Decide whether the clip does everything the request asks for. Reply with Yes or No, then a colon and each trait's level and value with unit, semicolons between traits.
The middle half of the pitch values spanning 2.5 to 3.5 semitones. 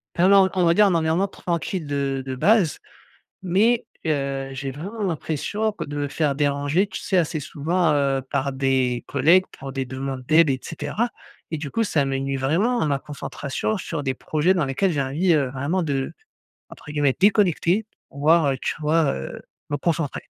No: average, 4.7 semitones